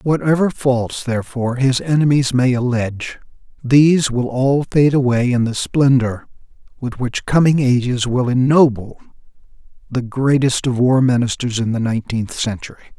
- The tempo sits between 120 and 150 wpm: Yes, average, 140 wpm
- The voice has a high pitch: No, low, 125 Hz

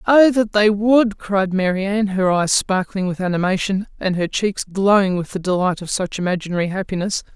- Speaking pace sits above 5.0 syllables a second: Yes, 5.2 syllables/s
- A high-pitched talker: Yes, high, 195 Hz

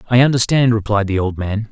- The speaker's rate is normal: No, fast, 210 wpm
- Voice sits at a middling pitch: No, low, 110 Hz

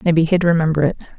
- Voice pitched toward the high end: No, medium, 165 Hz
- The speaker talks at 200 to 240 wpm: Yes, fast, 205 wpm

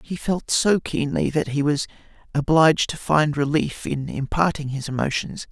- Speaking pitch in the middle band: Yes, medium, 145 Hz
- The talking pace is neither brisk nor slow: Yes, average, 165 wpm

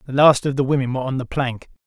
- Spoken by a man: Yes, male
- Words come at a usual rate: No, fast, 290 wpm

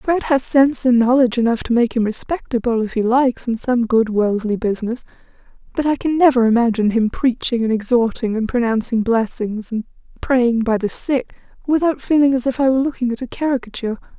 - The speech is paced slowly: No, average, 190 wpm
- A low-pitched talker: No, high, 240 Hz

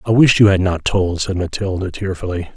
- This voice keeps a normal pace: No, fast, 210 wpm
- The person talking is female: No, male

